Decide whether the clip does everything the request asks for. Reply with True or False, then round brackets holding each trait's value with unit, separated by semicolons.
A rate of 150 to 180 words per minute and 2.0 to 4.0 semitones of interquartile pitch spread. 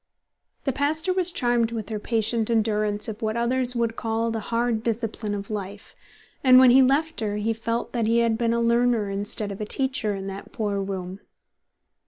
False (195 wpm; 2.5 semitones)